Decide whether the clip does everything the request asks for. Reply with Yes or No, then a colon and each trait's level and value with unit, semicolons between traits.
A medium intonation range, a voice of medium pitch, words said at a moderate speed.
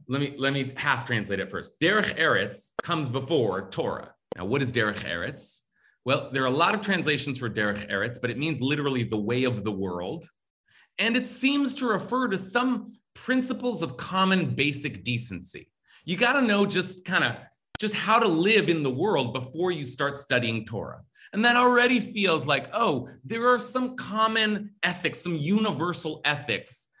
No: wide, 8.7 semitones; medium, 170 Hz; average, 180 wpm